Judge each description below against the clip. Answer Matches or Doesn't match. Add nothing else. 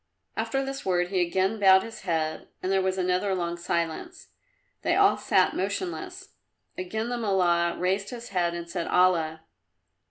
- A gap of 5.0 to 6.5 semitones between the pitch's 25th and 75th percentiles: Doesn't match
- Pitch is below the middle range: Doesn't match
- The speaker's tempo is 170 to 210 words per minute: Doesn't match